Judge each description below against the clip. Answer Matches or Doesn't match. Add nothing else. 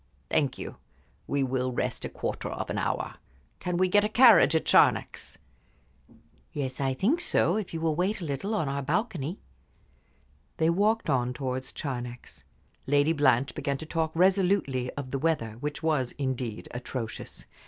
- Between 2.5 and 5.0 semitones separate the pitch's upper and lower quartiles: Doesn't match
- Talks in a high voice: Doesn't match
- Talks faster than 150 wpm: Matches